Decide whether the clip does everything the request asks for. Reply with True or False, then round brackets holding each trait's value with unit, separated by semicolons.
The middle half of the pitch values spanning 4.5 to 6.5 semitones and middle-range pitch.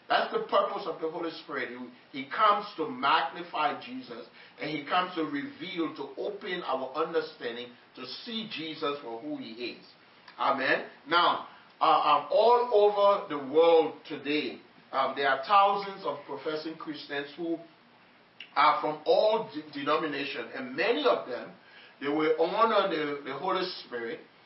True (5.6 semitones; 160 Hz)